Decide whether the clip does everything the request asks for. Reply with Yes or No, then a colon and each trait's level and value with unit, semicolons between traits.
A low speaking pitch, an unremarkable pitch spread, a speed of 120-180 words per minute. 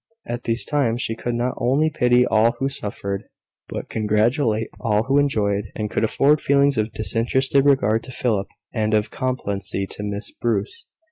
Yes: low, 115 Hz; average, 3.9 semitones; average, 165 wpm